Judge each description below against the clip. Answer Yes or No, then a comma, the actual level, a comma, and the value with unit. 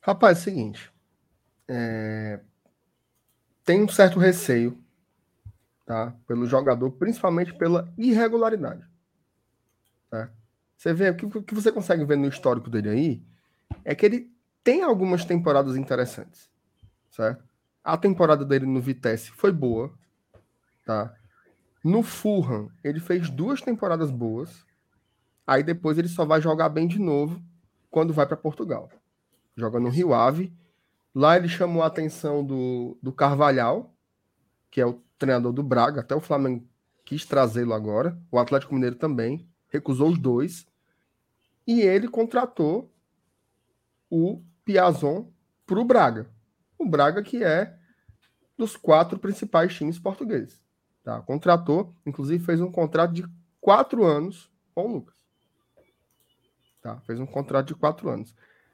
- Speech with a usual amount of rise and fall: No, wide, 6.3 semitones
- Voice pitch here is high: No, medium, 145 Hz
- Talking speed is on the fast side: No, average, 135 wpm